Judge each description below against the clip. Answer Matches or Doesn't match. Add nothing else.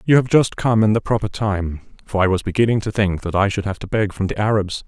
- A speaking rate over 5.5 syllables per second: Matches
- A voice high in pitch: Doesn't match